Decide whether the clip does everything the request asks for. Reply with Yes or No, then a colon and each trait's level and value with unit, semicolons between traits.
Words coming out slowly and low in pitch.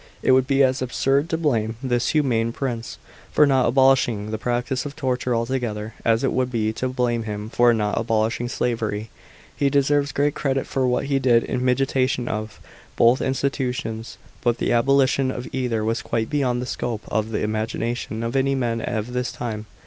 No: average, 185 wpm; low, 125 Hz